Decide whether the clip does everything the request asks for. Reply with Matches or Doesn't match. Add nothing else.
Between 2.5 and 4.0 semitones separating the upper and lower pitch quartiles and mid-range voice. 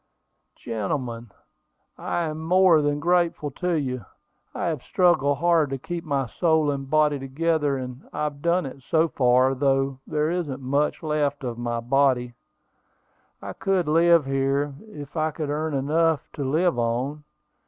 Matches